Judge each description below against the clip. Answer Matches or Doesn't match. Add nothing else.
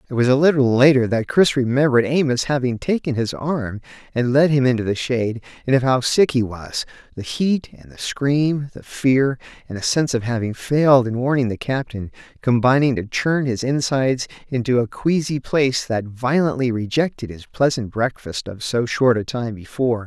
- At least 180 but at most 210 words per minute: Matches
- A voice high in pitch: Doesn't match